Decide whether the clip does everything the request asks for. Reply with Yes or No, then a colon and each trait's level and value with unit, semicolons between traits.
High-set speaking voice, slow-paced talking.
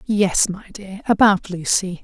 Yes: high, 195 Hz; slow, 120 wpm